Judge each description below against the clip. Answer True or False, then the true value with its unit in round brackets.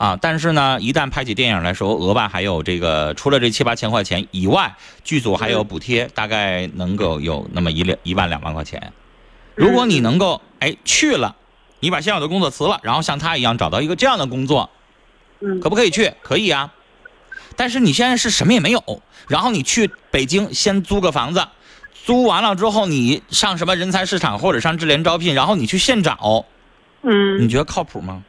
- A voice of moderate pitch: True (150 Hz)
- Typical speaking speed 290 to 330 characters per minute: True (310 characters per minute)